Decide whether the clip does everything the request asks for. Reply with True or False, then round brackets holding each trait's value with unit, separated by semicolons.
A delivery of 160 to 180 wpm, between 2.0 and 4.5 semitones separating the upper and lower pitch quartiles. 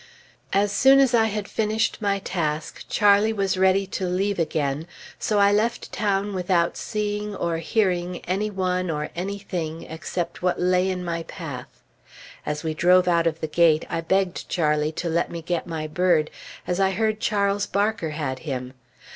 True (175 wpm; 3.5 semitones)